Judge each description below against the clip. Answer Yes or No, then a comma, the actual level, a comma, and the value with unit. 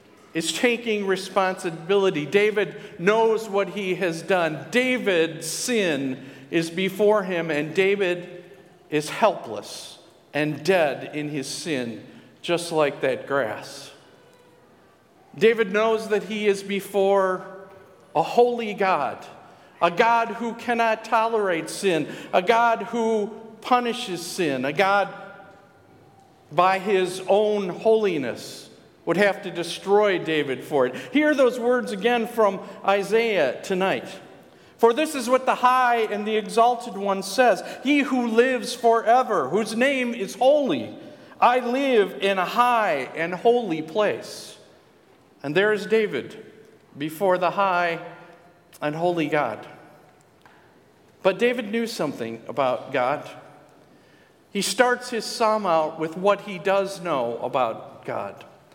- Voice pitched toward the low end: No, high, 200 Hz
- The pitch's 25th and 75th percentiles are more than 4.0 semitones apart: Yes, average, 4.7 semitones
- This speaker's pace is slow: Yes, slow, 125 wpm